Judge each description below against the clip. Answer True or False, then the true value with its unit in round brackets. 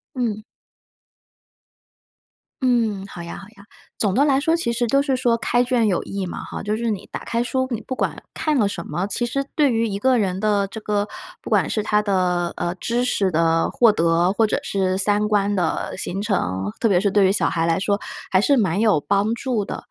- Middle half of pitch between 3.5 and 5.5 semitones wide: True (3.9 semitones)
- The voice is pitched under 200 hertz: False (210 Hz)